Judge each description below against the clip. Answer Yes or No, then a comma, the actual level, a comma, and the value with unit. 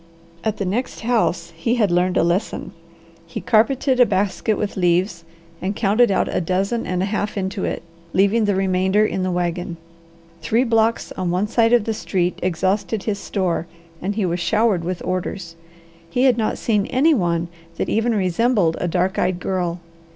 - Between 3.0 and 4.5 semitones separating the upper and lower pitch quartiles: Yes, average, 3.6 semitones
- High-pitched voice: Yes, high, 195 Hz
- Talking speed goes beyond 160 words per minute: Yes, average, 180 wpm